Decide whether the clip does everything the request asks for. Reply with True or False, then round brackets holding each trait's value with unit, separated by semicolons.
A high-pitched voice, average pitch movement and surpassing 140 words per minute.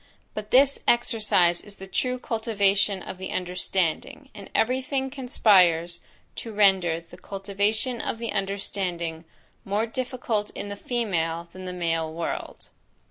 False (200 Hz; 4.3 semitones; 135 wpm)